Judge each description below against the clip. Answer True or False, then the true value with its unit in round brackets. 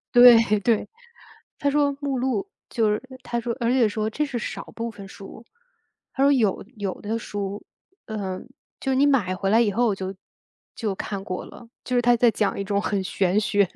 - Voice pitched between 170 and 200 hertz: False (220 Hz)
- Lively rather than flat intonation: False (3.5 semitones)